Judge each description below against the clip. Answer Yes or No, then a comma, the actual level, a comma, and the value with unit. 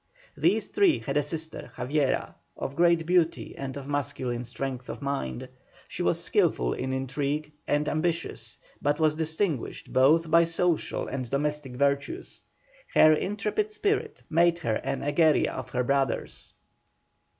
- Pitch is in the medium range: Yes, medium, 145 Hz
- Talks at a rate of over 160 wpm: No, average, 140 wpm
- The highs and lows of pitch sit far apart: No, average, 3.5 semitones